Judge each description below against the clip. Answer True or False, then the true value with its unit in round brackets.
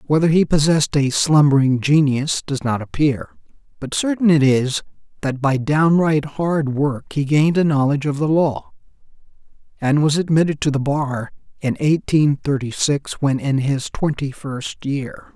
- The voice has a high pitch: False (145 Hz)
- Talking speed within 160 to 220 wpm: True (165 wpm)